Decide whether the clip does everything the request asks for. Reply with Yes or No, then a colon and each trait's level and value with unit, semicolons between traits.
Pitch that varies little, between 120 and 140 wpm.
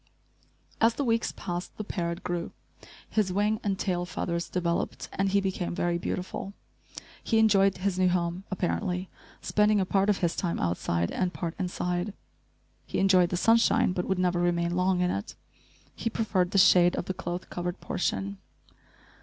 No: narrow, 2.1 semitones; average, 170 wpm